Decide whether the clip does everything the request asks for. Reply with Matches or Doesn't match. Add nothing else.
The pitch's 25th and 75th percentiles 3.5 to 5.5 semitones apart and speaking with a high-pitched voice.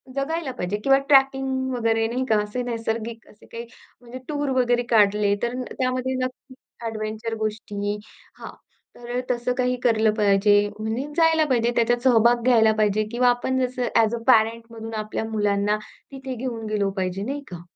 Doesn't match